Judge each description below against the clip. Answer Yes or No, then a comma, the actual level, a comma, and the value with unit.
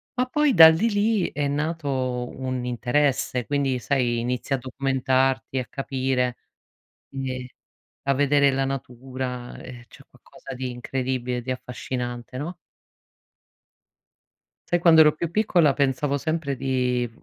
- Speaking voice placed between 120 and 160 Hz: Yes, low, 135 Hz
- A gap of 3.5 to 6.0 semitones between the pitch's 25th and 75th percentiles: No, average, 2.7 semitones